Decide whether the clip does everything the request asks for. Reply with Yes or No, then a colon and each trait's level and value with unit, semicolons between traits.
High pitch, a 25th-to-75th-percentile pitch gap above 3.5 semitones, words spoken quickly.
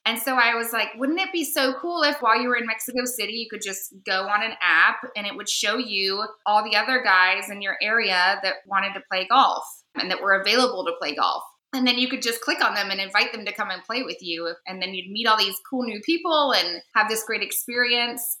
Yes: high, 215 Hz; average, 4.1 semitones; fast, 260 wpm